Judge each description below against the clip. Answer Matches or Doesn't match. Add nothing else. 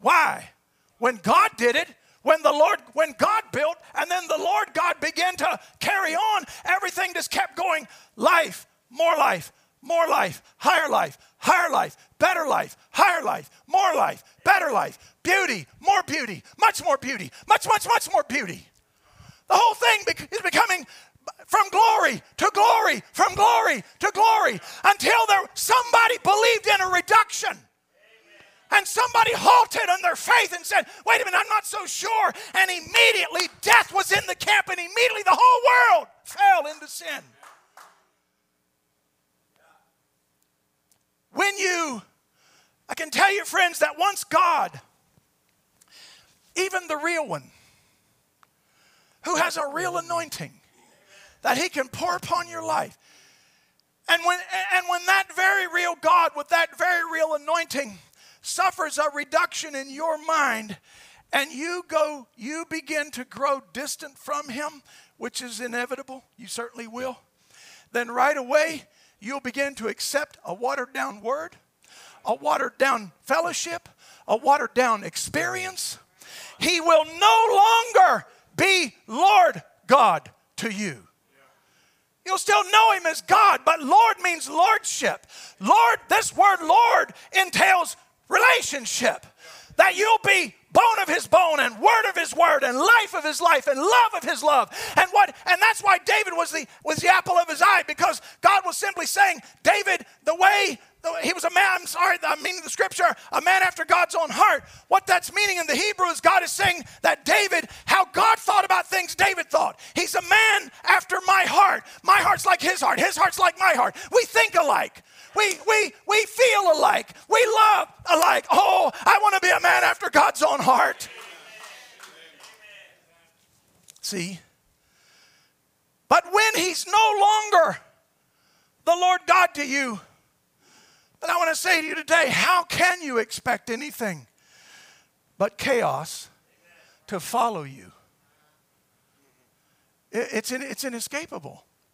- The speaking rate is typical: Matches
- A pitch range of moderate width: Matches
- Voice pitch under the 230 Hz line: Doesn't match